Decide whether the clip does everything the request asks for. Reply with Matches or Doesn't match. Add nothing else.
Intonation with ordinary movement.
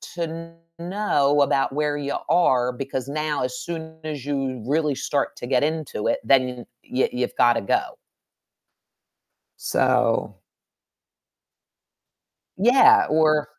Matches